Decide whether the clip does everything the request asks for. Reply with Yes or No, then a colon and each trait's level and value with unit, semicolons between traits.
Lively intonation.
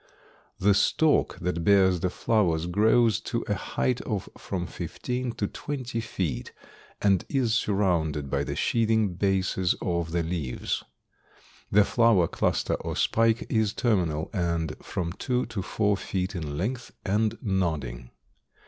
No: average, 4.7 semitones